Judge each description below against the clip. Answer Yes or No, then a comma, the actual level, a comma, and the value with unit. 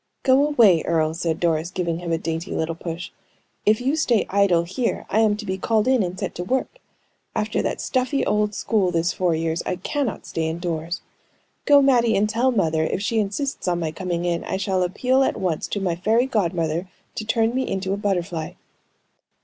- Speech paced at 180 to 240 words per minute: Yes, average, 200 wpm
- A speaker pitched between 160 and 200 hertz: Yes, high, 190 Hz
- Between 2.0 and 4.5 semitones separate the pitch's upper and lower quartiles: No, average, 5.0 semitones